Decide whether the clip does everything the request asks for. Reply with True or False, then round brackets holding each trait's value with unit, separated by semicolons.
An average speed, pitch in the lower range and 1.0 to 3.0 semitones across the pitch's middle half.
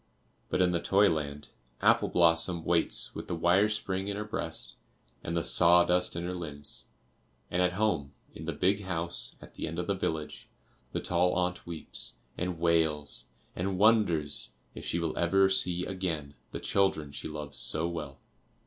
True (175 wpm; 85 Hz; 2.4 semitones)